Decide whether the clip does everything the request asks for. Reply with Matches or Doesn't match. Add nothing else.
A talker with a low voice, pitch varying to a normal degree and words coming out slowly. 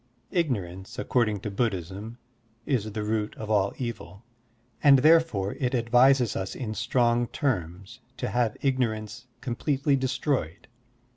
Matches